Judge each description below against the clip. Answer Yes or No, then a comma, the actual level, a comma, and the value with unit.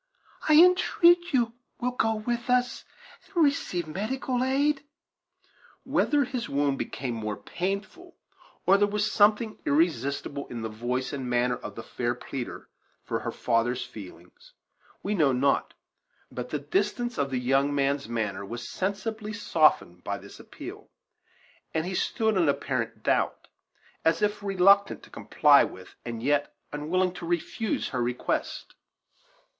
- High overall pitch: No, medium, 165 Hz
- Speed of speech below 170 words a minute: Yes, average, 145 wpm